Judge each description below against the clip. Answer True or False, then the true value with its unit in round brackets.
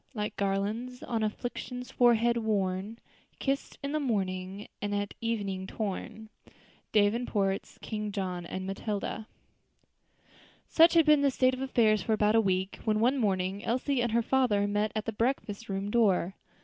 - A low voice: False (215 Hz)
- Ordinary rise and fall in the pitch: True (3.3 semitones)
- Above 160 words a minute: False (155 wpm)